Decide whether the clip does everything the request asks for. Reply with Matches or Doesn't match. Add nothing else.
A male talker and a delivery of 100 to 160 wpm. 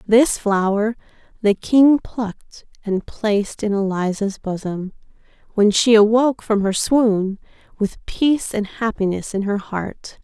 Doesn't match